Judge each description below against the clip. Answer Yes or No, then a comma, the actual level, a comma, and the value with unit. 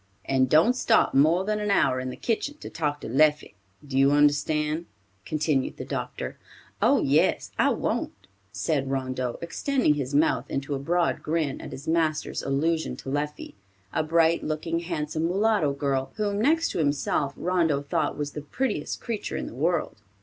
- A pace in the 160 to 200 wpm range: Yes, average, 170 wpm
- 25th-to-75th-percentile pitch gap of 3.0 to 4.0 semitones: Yes, average, 3.4 semitones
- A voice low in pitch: No, medium, 155 Hz